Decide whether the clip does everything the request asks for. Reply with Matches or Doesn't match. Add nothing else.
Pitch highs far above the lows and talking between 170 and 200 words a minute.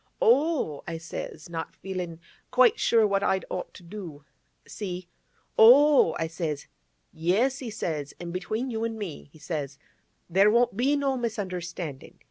Doesn't match